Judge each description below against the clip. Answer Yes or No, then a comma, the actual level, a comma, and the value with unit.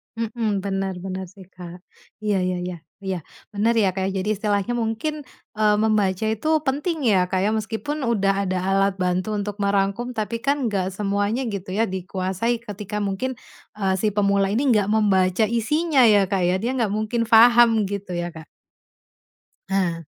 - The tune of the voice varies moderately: Yes, average, 3.0 semitones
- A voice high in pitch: Yes, high, 205 Hz